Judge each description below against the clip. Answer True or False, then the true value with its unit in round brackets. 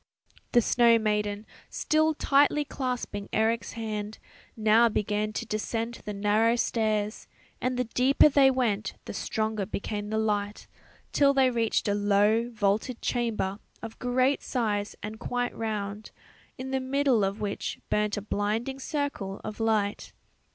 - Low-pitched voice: False (220 Hz)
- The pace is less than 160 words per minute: True (145 wpm)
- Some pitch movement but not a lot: True (3.1 semitones)